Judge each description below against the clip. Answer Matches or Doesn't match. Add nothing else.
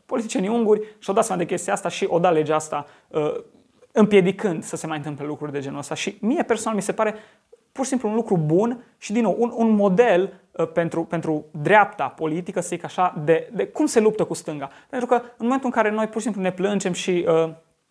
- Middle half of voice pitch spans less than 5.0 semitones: Doesn't match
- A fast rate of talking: Matches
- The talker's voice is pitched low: Doesn't match